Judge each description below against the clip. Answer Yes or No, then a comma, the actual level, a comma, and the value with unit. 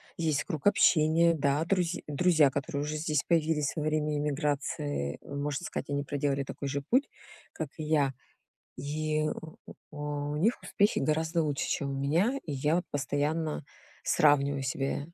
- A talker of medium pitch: Yes, medium, 150 Hz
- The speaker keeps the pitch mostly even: Yes, narrow, 2.0 semitones